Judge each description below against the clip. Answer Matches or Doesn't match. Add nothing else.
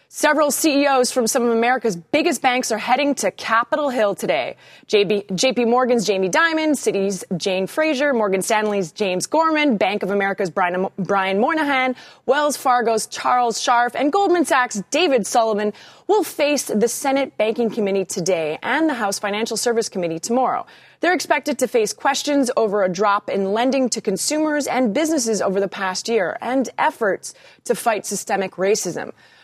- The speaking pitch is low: Doesn't match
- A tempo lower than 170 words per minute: Matches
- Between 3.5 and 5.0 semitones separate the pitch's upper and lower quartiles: Doesn't match